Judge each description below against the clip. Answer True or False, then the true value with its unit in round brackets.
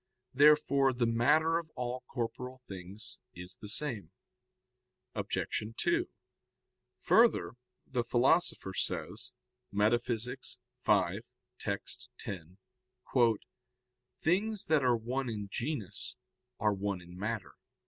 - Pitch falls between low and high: False (120 Hz)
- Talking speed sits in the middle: False (100 wpm)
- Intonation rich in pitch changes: True (5.8 semitones)